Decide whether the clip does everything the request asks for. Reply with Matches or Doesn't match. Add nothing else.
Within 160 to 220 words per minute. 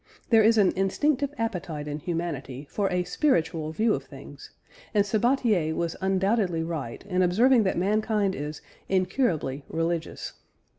Doesn't match